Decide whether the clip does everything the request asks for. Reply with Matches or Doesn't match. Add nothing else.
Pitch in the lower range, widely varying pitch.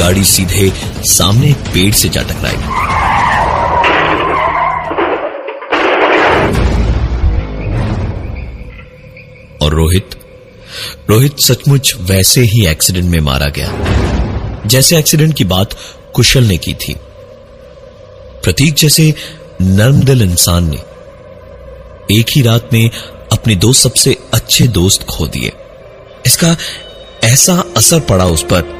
Matches